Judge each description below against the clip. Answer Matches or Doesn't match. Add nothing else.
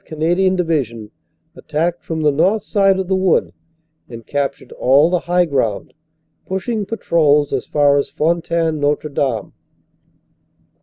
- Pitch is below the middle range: Doesn't match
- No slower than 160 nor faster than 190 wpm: Doesn't match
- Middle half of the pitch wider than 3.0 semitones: Matches